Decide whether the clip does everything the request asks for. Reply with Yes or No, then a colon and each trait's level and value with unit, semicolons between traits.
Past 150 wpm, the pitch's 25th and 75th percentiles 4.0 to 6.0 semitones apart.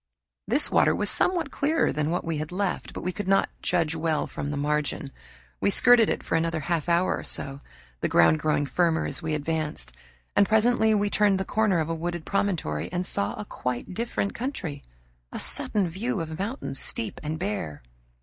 Yes: average, 195 wpm; average, 5.0 semitones